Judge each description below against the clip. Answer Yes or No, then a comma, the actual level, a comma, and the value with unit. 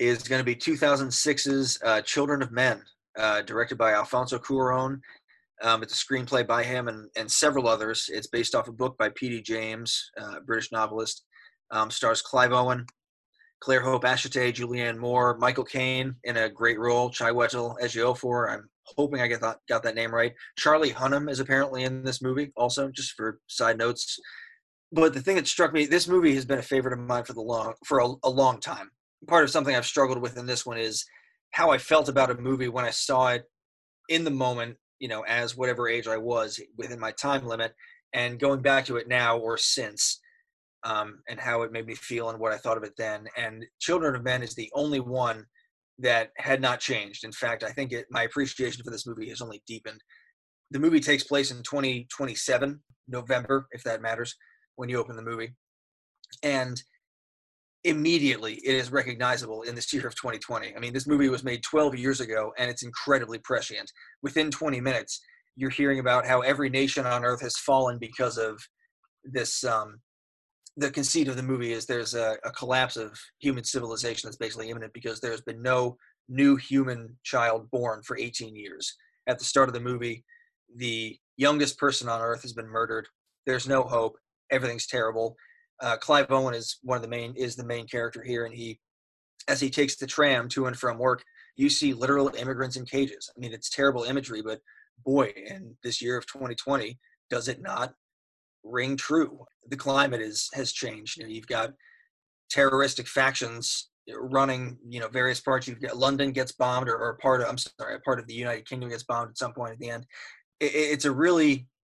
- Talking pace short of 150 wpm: No, average, 200 wpm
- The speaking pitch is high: No, low, 125 Hz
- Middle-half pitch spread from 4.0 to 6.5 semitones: No, average, 2.8 semitones